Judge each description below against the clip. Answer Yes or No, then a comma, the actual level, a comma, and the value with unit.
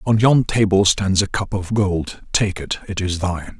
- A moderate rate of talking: No, fast, 215 wpm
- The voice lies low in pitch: Yes, low, 100 Hz